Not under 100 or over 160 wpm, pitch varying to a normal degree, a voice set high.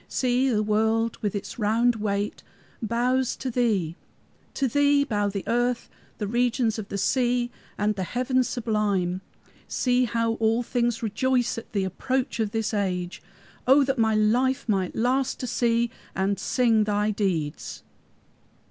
Yes: average, 150 wpm; average, 3.1 semitones; high, 225 Hz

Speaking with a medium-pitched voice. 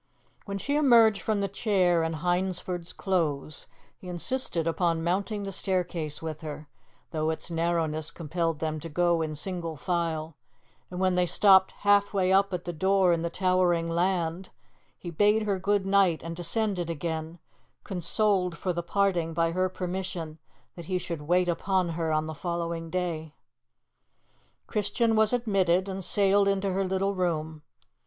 Yes: medium, 180 Hz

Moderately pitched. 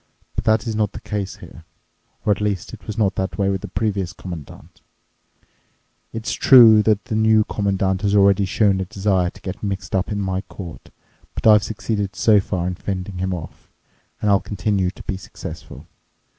No: low, 100 Hz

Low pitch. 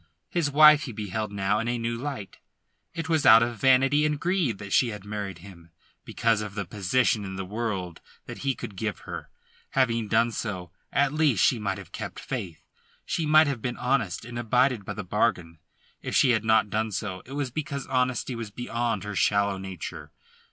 Yes: low, 115 Hz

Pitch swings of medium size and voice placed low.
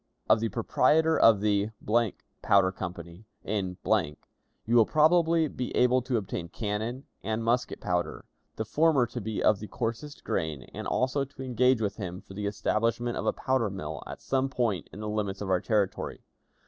Yes: average, 4.2 semitones; low, 110 Hz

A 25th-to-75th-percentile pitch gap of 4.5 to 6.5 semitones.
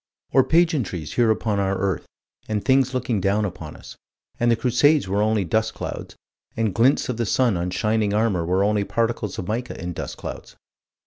No: average, 3.7 semitones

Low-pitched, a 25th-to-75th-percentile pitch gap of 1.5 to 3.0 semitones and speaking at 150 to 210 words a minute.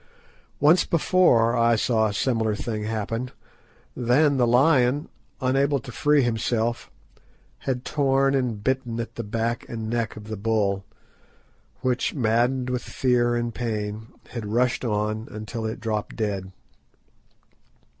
No: low, 120 Hz; narrow, 2.6 semitones; slow, 135 wpm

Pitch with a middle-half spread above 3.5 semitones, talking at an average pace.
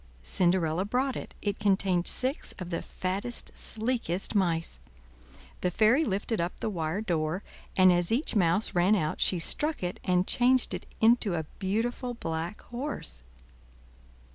Yes: average, 4.8 semitones; average, 145 wpm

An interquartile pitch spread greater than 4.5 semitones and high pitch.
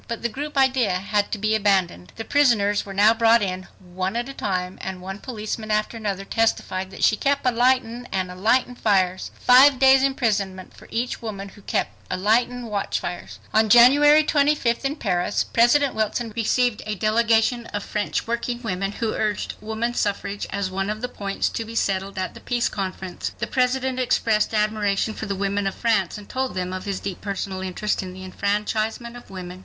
No: average, 3.6 semitones; high, 215 Hz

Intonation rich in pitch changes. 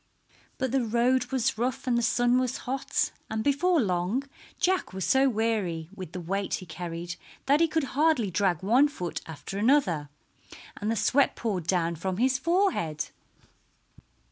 Yes: wide, 6.7 semitones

